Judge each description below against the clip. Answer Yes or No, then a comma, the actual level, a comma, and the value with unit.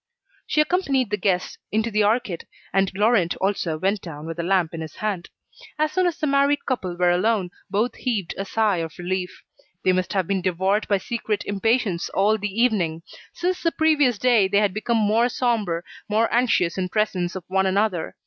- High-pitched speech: Yes, high, 205 Hz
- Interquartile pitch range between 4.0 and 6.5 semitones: Yes, average, 4.3 semitones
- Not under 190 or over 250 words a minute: Yes, average, 195 wpm